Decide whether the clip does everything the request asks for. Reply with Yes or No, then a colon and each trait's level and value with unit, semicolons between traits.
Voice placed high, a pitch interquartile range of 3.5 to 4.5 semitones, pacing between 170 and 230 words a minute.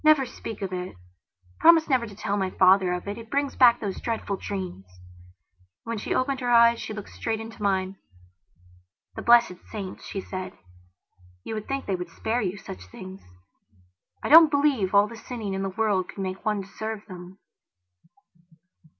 Yes: high, 205 Hz; average, 3.8 semitones; average, 180 wpm